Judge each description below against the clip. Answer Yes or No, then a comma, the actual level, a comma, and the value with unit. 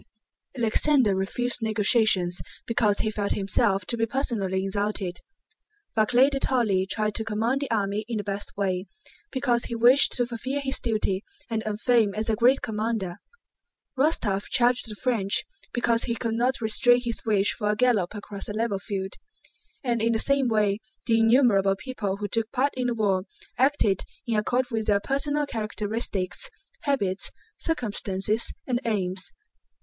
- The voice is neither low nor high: No, high, 220 Hz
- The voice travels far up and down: No, average, 3.3 semitones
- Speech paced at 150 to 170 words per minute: Yes, average, 160 wpm